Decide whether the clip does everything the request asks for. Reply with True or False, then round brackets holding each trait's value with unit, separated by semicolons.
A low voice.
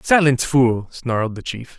True (125 Hz)